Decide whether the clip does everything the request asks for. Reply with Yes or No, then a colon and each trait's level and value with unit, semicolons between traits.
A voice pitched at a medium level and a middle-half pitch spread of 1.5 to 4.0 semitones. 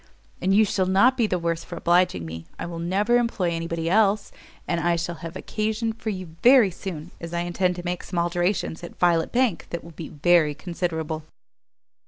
Yes: medium, 175 Hz; average, 2.9 semitones